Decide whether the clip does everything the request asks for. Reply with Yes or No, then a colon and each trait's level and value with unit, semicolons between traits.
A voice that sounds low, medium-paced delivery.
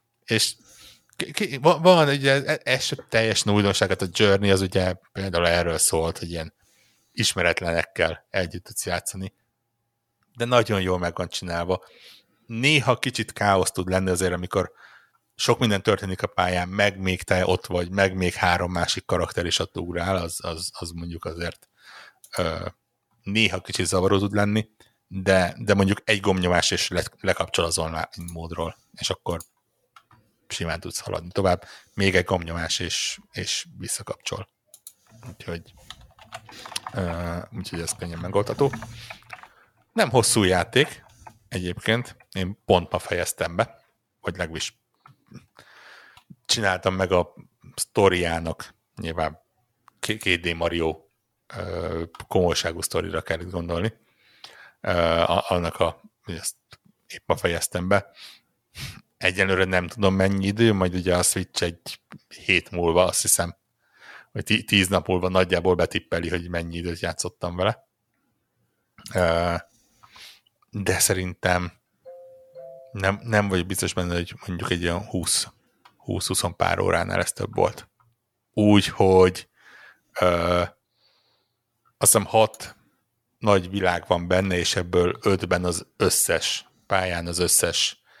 Yes: very low, 95 Hz; average, 120 wpm